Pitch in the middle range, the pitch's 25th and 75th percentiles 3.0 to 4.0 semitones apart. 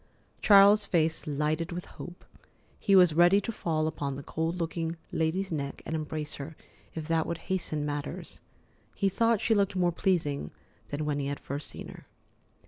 Yes: medium, 165 Hz; average, 3.5 semitones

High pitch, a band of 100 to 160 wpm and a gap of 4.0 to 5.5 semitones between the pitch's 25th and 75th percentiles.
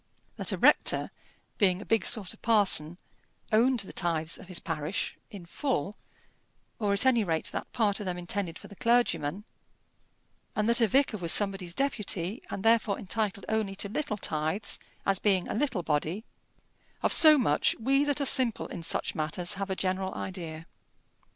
No: high, 200 Hz; average, 175 wpm; average, 4.4 semitones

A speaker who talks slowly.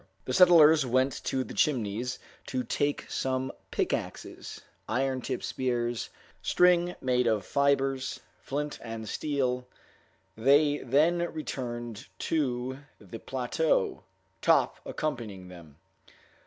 Yes: slow, 105 wpm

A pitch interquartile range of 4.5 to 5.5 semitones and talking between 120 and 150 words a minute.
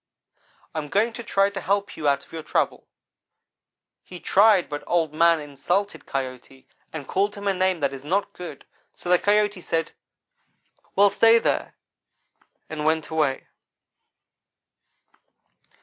Yes: average, 5.0 semitones; average, 145 wpm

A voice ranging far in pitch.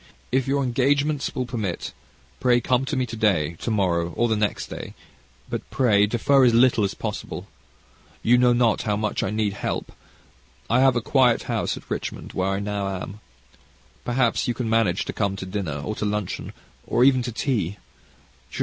No: average, 3.7 semitones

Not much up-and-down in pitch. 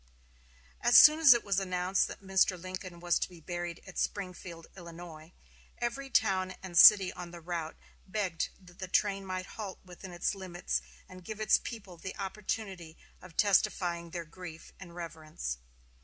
Yes: narrow, 2.2 semitones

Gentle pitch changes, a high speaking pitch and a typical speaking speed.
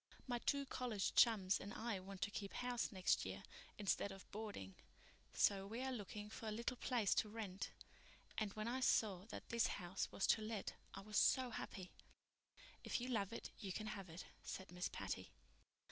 No: average, 3.2 semitones; high, 210 Hz; average, 190 wpm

